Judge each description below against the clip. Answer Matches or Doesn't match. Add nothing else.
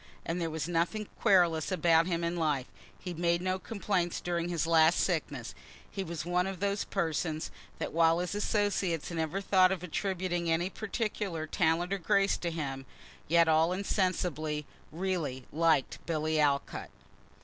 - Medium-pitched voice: Matches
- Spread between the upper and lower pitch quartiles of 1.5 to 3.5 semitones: Matches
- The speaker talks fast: Doesn't match